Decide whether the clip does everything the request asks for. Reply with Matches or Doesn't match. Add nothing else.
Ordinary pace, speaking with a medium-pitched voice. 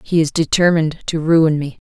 Matches